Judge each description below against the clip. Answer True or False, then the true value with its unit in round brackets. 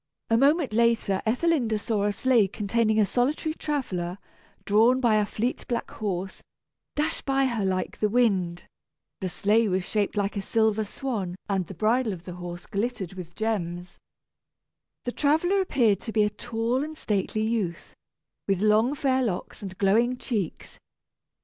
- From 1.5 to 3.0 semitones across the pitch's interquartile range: False (4.1 semitones)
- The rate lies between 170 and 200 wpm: False (160 wpm)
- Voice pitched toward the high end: True (215 Hz)